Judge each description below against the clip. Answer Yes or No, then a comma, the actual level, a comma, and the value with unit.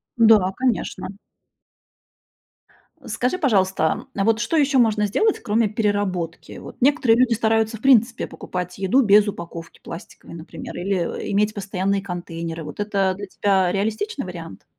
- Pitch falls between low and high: No, high, 205 Hz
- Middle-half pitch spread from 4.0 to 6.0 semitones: No, average, 3.5 semitones